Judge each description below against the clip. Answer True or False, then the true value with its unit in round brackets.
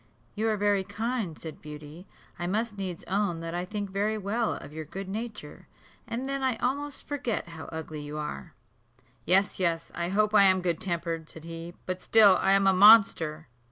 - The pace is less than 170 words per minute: False (190 wpm)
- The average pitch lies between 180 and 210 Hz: True (190 Hz)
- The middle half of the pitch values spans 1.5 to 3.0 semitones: False (4.3 semitones)